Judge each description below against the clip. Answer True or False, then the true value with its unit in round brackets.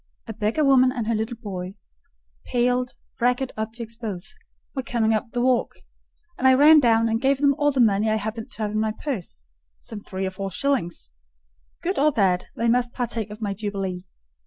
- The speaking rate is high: False (180 wpm)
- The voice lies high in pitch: True (225 Hz)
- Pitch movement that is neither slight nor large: True (4.0 semitones)